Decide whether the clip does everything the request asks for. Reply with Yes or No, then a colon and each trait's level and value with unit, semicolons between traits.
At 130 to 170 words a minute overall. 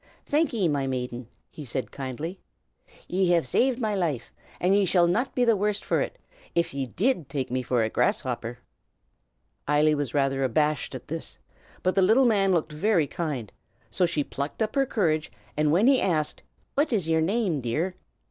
No: average, 190 wpm